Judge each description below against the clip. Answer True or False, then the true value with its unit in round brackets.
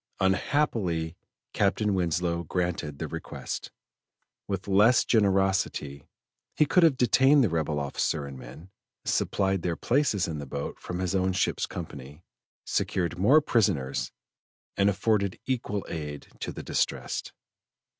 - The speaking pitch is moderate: False (95 Hz)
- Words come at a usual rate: False (130 wpm)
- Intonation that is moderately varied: True (4.5 semitones)